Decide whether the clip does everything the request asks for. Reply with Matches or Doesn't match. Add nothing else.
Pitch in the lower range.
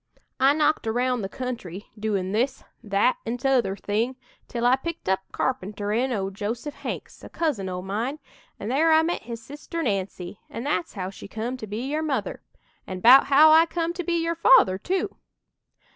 Doesn't match